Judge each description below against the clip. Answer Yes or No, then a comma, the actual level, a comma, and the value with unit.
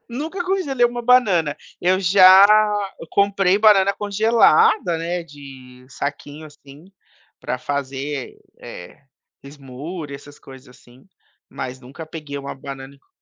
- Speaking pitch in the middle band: Yes, medium, 155 Hz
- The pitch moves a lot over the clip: Yes, wide, 6.3 semitones